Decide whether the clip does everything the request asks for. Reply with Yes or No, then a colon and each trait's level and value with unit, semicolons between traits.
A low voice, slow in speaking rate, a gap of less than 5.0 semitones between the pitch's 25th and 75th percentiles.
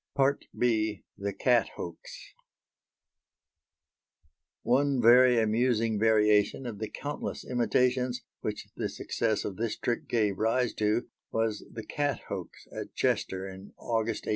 Yes: low, 115 Hz; slow, 125 wpm; narrow, 2.6 semitones